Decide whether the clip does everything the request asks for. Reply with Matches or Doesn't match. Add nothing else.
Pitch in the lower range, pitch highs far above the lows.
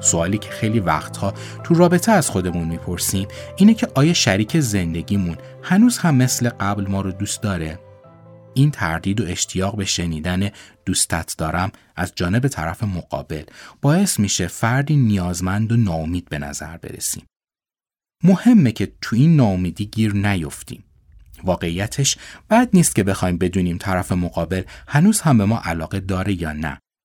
Matches